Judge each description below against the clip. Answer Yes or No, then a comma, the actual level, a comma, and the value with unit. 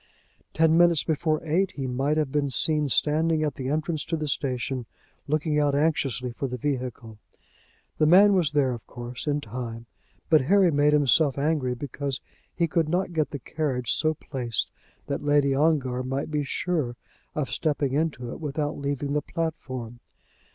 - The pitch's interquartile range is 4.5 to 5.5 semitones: No, average, 3.3 semitones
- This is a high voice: No, medium, 145 Hz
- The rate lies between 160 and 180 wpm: Yes, average, 170 wpm